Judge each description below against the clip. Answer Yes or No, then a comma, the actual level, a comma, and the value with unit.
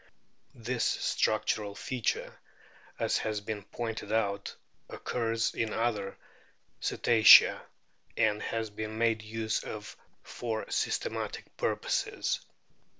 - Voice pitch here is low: Yes, low, 110 Hz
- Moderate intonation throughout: No, narrow, 1.3 semitones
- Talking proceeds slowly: Yes, slow, 95 wpm